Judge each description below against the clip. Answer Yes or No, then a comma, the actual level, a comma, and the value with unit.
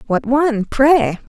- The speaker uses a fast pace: No, slow, 135 wpm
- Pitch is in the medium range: No, very high, 255 Hz